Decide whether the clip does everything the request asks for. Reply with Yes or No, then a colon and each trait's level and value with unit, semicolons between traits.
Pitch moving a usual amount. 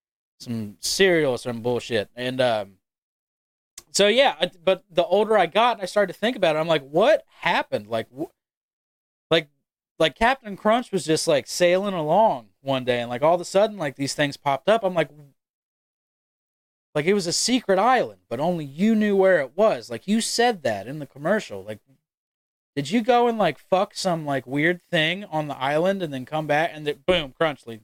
No: wide, 6.6 semitones